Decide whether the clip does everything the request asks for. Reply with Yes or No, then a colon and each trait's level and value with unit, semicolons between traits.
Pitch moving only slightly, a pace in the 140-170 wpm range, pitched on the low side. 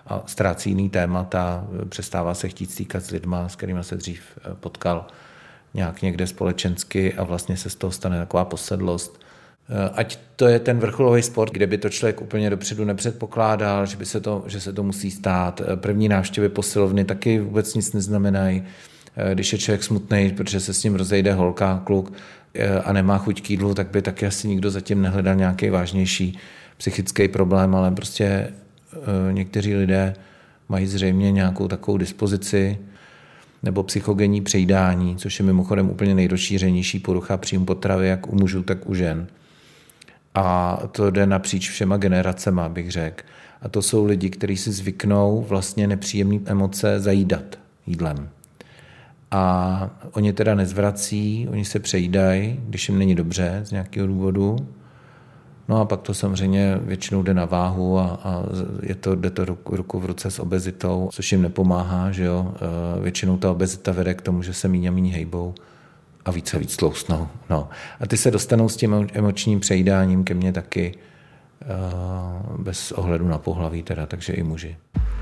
Yes: narrow, 1.7 semitones; average, 165 wpm; very low, 95 Hz